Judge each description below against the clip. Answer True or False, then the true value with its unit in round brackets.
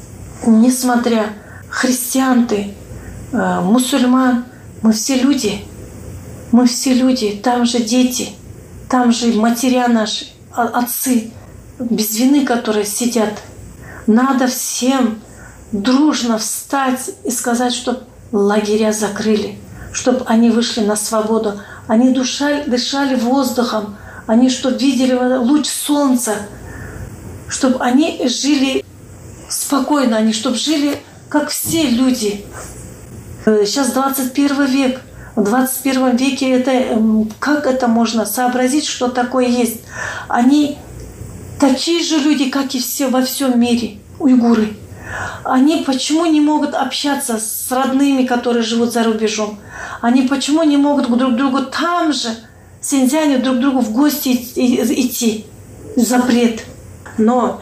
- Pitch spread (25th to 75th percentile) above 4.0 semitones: False (2.9 semitones)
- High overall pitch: True (250 Hz)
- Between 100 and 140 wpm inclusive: True (115 wpm)